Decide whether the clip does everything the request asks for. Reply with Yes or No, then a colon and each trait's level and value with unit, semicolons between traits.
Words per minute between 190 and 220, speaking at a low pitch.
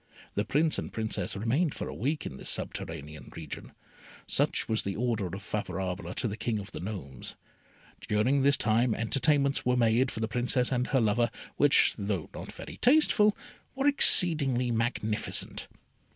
No: average, 165 wpm; low, 115 Hz